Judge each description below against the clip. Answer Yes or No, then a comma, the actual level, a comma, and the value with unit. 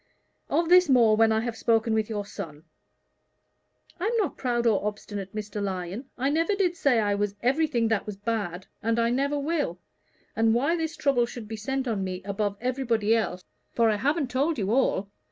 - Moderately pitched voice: No, high, 230 Hz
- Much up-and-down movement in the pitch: No, average, 4.7 semitones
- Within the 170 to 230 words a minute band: Yes, average, 190 wpm